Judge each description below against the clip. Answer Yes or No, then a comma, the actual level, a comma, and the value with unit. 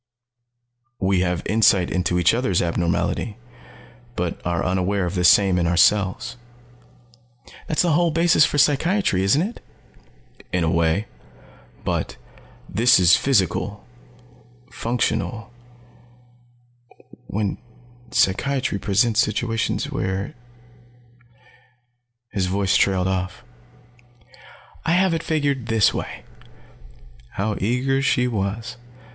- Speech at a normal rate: No, slow, 105 wpm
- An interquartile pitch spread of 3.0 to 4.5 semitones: No, average, 5.0 semitones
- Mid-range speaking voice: No, low, 105 Hz